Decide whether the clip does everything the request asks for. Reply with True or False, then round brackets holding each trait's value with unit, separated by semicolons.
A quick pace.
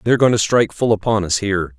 True (270 wpm)